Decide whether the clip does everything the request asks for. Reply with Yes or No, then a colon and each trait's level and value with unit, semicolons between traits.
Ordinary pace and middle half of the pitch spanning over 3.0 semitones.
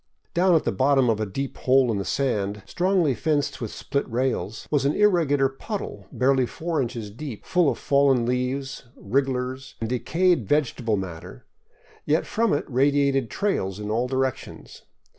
Yes: average, 160 wpm; average, 3.8 semitones